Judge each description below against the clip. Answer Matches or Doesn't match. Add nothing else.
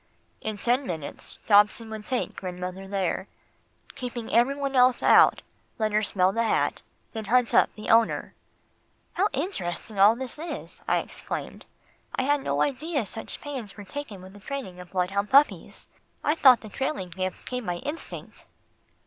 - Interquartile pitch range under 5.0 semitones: Doesn't match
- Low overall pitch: Doesn't match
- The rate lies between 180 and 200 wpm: Doesn't match